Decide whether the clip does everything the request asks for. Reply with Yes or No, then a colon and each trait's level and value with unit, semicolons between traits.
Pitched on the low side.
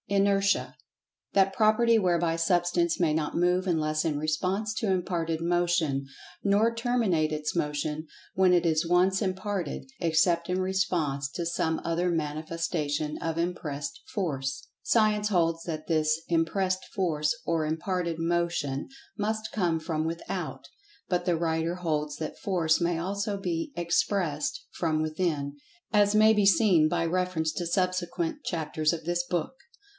No: medium, 170 Hz